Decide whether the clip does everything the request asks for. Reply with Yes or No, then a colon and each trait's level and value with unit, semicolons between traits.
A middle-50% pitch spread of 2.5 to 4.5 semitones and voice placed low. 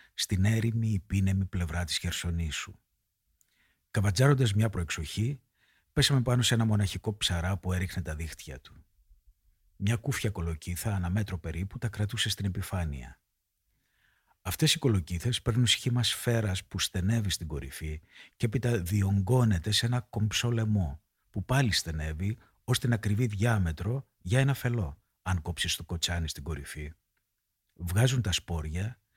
No: average, 5.1 semitones; low, 100 Hz